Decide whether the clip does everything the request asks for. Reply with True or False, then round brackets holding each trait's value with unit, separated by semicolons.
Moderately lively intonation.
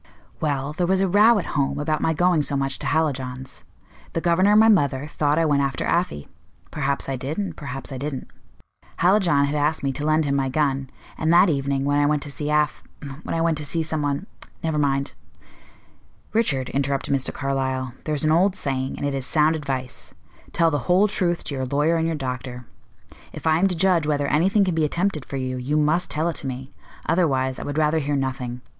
True (3.2 semitones)